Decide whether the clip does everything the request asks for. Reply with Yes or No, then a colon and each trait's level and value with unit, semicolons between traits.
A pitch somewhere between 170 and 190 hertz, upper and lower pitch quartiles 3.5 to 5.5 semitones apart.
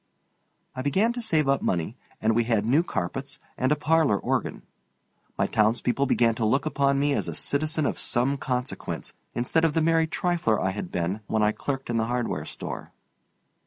No: low, 135 Hz; average, 5.2 semitones